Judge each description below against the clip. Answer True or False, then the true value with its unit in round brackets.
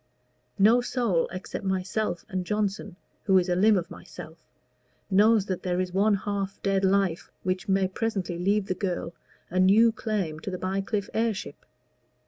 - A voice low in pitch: False (195 Hz)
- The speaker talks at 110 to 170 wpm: True (160 wpm)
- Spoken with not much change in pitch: True (2.2 semitones)